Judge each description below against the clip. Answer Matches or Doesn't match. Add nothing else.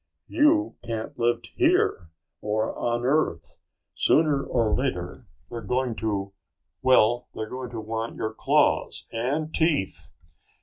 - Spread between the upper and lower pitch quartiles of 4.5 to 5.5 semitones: Doesn't match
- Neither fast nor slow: Doesn't match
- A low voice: Matches